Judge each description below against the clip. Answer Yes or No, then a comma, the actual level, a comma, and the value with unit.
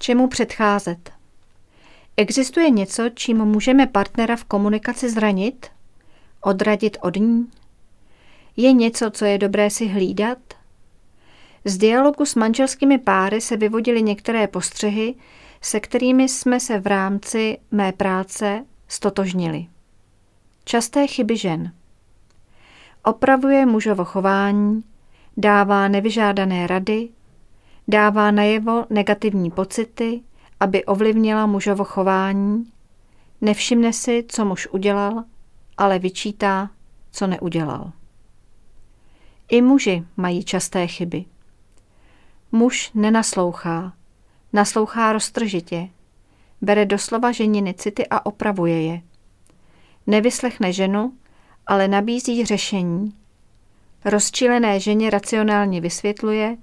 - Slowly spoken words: Yes, slow, 95 wpm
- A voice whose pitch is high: Yes, high, 205 Hz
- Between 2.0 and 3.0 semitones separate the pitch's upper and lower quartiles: No, average, 3.7 semitones